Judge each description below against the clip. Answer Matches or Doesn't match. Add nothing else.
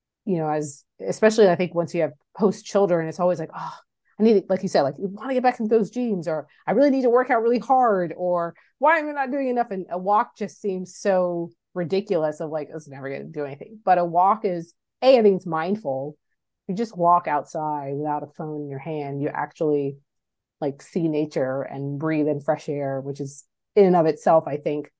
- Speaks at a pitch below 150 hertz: Doesn't match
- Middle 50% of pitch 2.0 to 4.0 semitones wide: Doesn't match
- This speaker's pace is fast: Matches